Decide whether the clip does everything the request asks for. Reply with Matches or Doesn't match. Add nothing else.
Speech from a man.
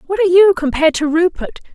Doesn't match